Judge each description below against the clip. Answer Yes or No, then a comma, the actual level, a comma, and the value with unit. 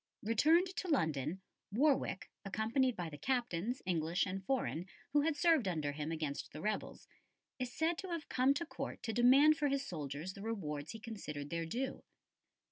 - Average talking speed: Yes, average, 175 wpm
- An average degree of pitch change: No, wide, 8.8 semitones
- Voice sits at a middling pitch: No, high, 220 Hz